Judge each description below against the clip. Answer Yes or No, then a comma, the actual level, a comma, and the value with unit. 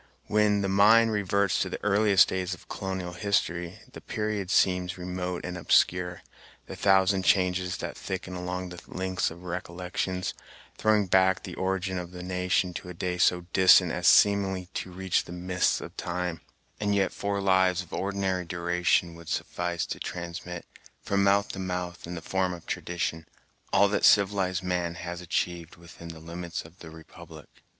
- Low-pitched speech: Yes, very low, 90 Hz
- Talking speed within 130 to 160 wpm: No, average, 170 wpm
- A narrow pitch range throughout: Yes, narrow, 1.5 semitones